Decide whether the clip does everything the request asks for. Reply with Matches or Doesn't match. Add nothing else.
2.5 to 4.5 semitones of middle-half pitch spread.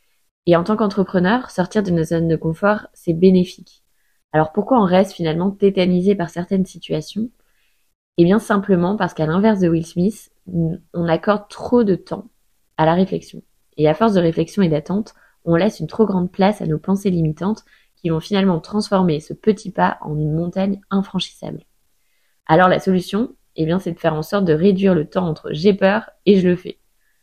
Matches